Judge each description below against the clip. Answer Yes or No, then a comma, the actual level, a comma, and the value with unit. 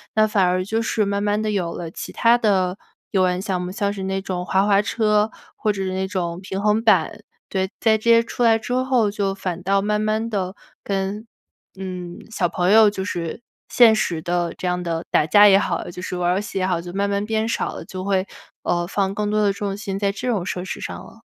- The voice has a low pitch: No, high, 195 Hz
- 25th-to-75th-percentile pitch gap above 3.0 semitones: No, narrow, 2.6 semitones